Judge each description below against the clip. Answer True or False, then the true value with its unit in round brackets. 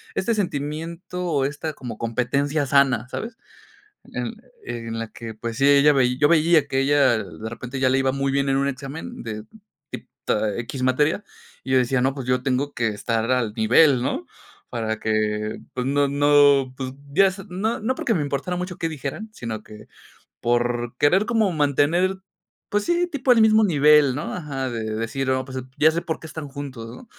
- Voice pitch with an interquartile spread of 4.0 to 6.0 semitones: True (4.3 semitones)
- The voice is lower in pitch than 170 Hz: True (140 Hz)